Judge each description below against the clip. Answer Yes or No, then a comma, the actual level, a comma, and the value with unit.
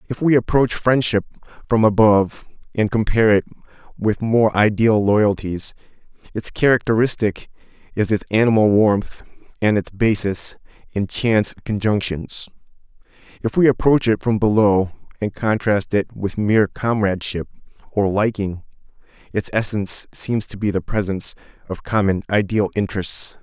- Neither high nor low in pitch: No, low, 105 Hz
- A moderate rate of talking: No, slow, 130 wpm